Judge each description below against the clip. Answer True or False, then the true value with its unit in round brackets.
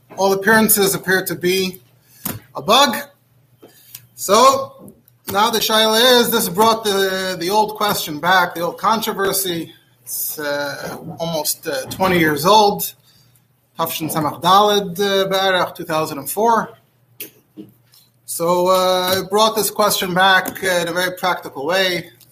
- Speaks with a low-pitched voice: False (185 Hz)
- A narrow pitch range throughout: False (5.2 semitones)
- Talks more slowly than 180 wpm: True (135 wpm)